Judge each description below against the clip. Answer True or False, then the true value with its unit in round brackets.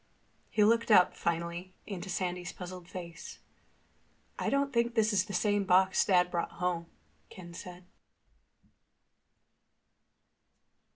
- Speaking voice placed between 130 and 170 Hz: False (185 Hz)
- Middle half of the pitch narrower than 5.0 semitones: True (2.6 semitones)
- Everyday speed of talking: False (115 wpm)